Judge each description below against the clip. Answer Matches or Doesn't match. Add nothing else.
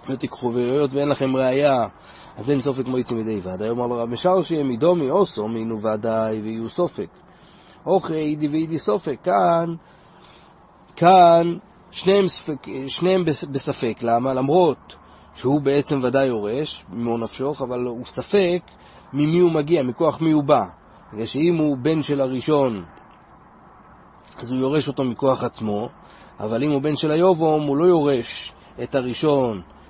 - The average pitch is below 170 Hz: Matches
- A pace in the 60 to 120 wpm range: Doesn't match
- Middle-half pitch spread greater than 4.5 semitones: Matches